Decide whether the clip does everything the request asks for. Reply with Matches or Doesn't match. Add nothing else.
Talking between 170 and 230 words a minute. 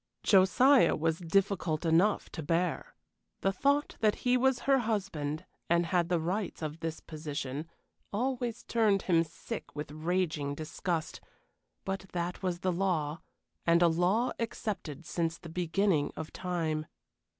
Doesn't match